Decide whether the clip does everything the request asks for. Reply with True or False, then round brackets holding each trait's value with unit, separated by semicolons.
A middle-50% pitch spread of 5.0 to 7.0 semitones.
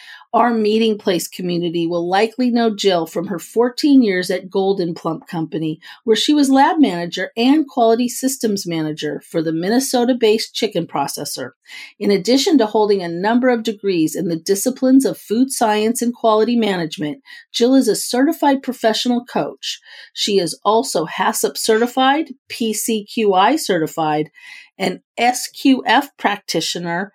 True (5.6 semitones)